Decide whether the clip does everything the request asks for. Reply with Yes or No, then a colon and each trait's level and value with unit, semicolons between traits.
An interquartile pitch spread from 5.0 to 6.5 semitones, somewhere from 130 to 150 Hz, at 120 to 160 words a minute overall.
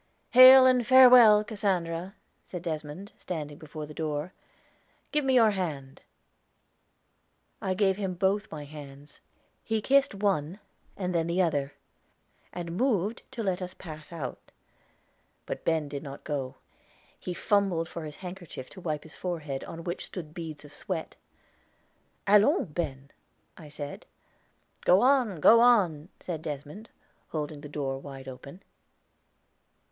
No: average, 5.3 semitones; medium, 170 Hz; average, 140 wpm